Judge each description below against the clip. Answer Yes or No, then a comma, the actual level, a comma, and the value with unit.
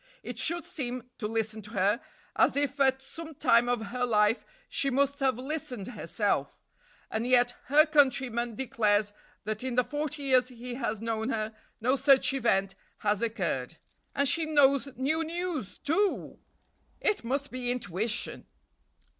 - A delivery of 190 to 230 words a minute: No, average, 155 wpm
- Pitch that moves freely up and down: No, average, 4.0 semitones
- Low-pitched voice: No, very high, 250 Hz